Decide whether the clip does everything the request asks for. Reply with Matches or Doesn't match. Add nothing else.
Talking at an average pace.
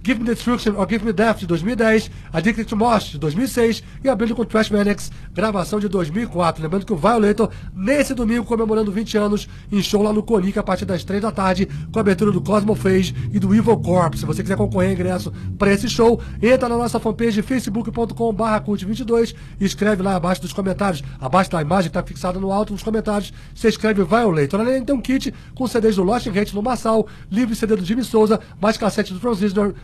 Doesn't match